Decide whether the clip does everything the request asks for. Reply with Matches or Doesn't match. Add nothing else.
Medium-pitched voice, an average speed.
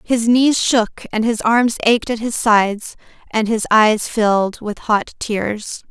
Doesn't match